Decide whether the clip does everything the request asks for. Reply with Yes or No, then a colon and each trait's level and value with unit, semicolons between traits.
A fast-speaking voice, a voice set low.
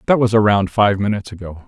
Yes: fast, 215 wpm; low, 105 Hz